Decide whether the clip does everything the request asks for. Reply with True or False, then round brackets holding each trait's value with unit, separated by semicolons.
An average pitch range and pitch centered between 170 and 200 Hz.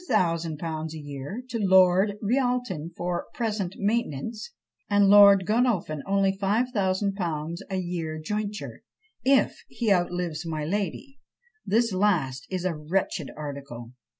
True (4.6 semitones; 185 Hz)